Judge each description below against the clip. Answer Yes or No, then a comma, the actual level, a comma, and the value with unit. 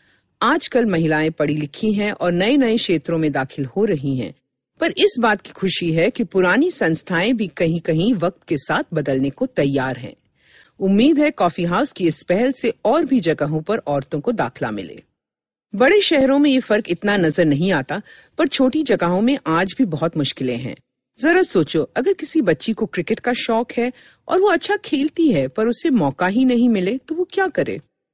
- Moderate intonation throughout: No, wide, 8.1 semitones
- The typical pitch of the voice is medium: No, high, 205 Hz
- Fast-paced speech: Yes, fast, 195 wpm